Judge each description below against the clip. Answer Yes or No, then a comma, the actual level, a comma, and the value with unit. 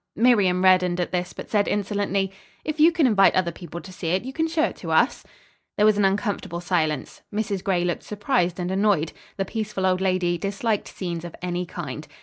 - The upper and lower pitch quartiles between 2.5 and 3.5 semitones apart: Yes, average, 2.9 semitones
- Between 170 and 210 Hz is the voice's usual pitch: Yes, high, 190 Hz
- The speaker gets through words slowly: No, fast, 205 wpm